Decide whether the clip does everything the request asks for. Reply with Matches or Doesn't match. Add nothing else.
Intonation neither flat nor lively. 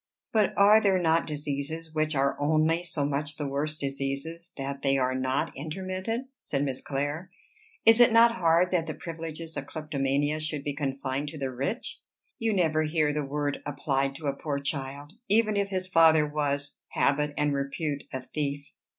Matches